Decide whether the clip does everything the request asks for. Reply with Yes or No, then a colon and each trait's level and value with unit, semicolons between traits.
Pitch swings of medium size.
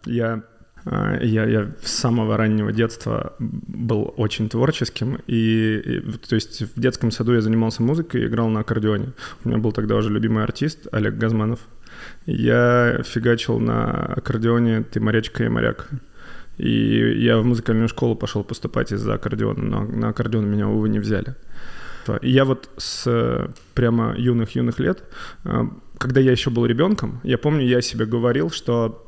No: narrow, 1.9 semitones